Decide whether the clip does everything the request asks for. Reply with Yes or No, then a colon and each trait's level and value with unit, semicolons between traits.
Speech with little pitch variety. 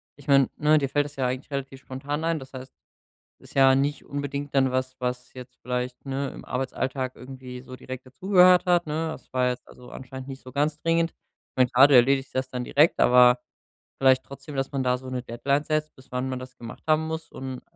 Yes: narrow, 2.1 semitones